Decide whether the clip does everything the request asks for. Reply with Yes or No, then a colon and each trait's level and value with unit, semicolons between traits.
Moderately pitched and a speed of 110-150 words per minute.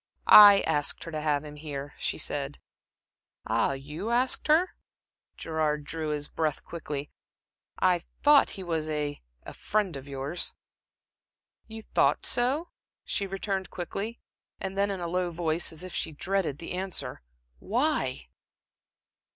Yes: medium, 170 Hz; average, 145 wpm